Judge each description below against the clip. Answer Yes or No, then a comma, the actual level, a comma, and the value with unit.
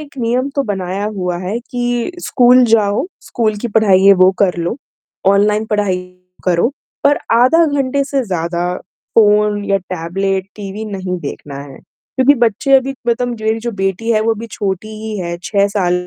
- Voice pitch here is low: No, high, 210 Hz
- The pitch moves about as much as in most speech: Yes, average, 4.1 semitones